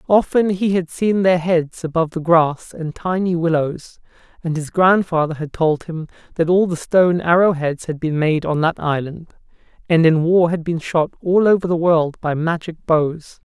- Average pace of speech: Yes, average, 190 wpm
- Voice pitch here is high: No, medium, 165 Hz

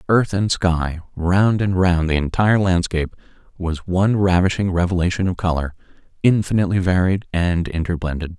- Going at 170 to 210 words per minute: No, slow, 135 wpm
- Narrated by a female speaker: No, male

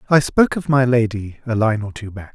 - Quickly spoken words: Yes, fast, 255 wpm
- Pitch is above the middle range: No, low, 120 Hz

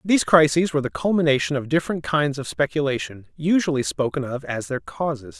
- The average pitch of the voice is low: No, medium, 145 Hz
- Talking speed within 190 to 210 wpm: No, average, 180 wpm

